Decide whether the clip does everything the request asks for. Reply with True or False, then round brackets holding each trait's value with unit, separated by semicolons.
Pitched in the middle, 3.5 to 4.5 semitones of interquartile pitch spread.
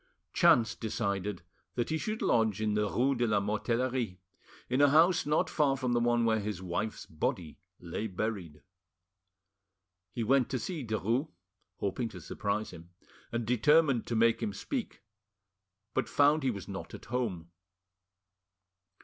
False (115 Hz; 4.2 semitones)